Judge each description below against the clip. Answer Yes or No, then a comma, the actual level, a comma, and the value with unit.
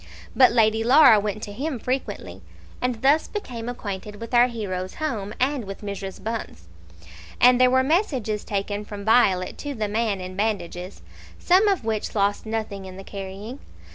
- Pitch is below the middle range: No, high, 220 Hz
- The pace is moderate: Yes, average, 170 wpm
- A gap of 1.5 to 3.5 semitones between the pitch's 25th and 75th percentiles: No, average, 4.0 semitones